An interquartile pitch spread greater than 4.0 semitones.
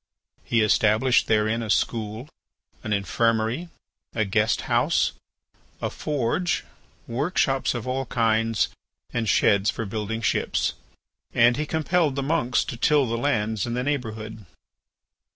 No: average, 3.5 semitones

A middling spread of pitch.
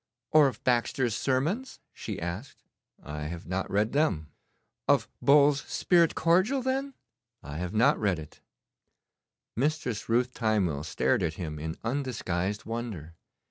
No: wide, 8.7 semitones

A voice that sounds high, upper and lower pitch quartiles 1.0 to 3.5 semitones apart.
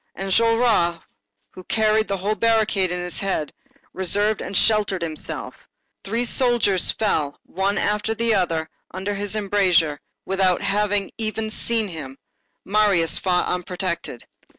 Yes: high, 195 Hz; average, 3.2 semitones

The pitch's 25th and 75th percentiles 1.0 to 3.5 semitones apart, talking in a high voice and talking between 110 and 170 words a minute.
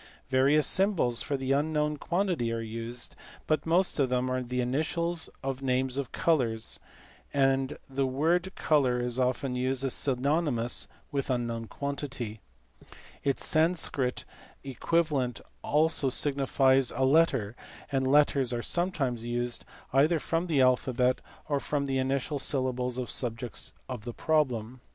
No: average, 3.1 semitones; low, 135 Hz; slow, 135 wpm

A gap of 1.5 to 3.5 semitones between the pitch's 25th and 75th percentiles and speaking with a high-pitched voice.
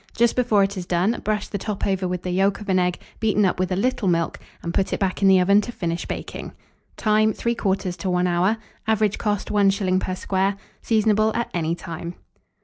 Yes: average, 2.7 semitones; high, 195 Hz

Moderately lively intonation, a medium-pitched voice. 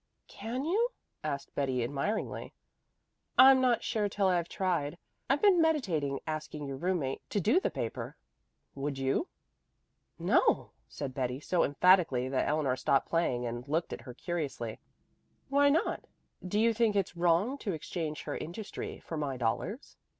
No: wide, 7.7 semitones; medium, 165 Hz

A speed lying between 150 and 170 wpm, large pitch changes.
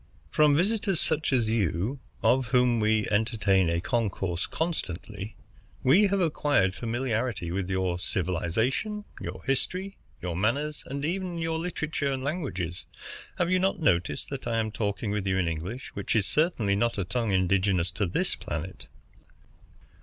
Yes: average, 155 wpm; wide, 7.8 semitones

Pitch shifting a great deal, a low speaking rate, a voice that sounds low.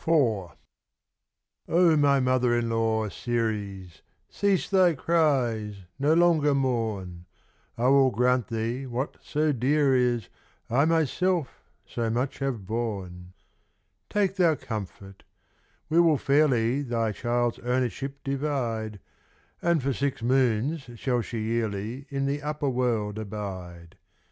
No: average, 4.4 semitones; slow, 120 wpm; low, 125 Hz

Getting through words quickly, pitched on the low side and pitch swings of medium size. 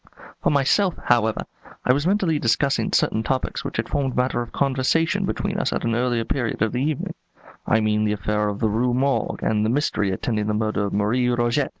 Yes: fast, 210 wpm; low, 120 Hz; average, 4.0 semitones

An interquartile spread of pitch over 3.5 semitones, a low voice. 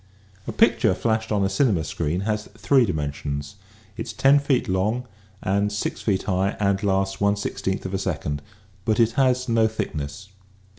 No: average, 3.0 semitones; low, 100 Hz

